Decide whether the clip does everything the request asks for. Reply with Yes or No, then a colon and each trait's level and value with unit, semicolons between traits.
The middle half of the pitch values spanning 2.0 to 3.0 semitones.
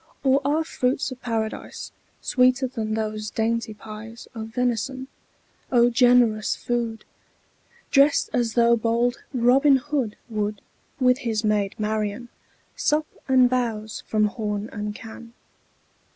Yes: average, 2.7 semitones